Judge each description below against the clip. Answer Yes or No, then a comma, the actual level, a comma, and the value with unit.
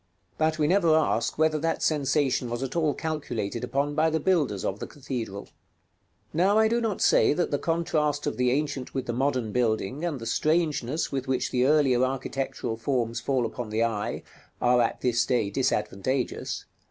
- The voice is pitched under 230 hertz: Yes, low, 135 Hz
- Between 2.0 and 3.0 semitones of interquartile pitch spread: No, average, 4.3 semitones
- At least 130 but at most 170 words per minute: No, average, 190 wpm